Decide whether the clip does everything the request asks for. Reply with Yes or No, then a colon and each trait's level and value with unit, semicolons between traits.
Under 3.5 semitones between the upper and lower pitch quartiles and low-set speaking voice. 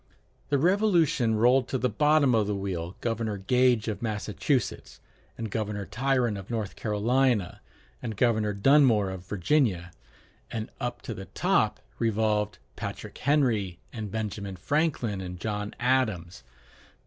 No: average, 4.0 semitones; low, 110 Hz